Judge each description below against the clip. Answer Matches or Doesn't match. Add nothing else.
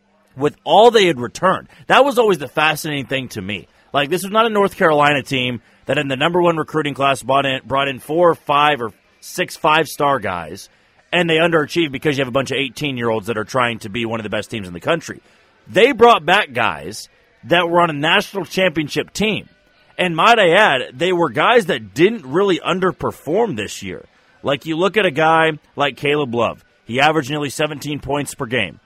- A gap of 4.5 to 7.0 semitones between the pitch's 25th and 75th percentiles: Matches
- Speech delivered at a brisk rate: Matches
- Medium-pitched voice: Matches